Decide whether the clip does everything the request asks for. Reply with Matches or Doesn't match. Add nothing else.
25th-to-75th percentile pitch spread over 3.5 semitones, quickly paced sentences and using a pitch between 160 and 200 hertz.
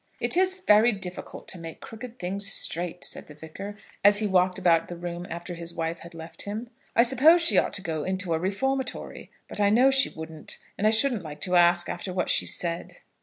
Matches